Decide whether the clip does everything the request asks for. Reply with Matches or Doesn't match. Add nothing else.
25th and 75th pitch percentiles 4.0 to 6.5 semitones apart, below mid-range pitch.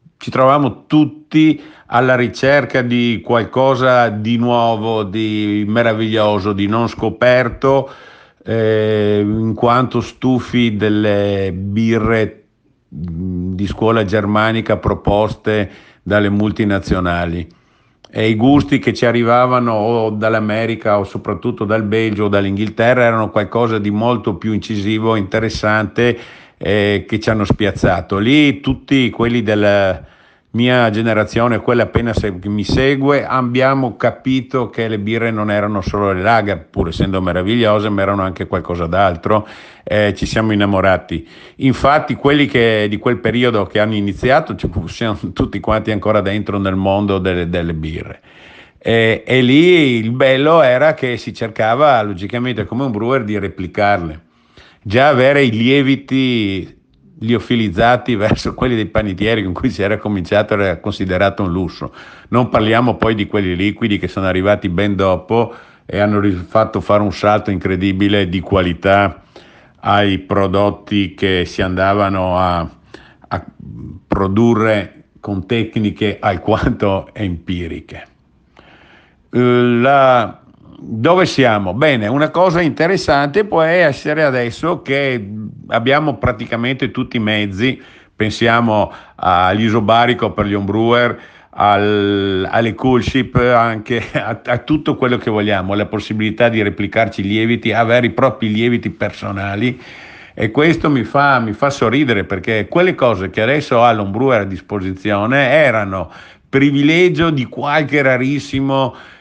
Doesn't match